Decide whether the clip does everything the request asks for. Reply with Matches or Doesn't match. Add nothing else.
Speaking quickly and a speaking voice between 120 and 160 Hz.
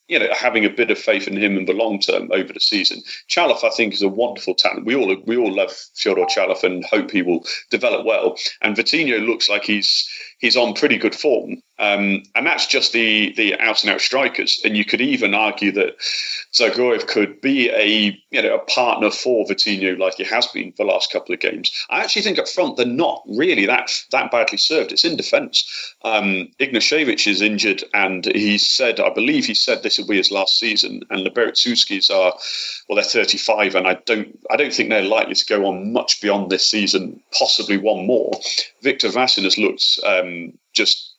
Doesn't match